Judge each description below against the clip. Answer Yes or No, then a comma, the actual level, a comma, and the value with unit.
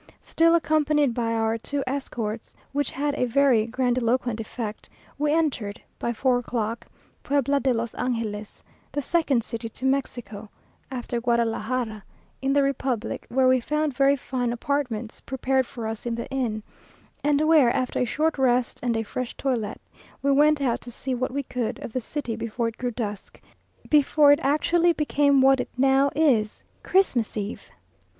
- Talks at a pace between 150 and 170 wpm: Yes, average, 165 wpm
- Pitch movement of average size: Yes, average, 3.4 semitones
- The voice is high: Yes, very high, 255 Hz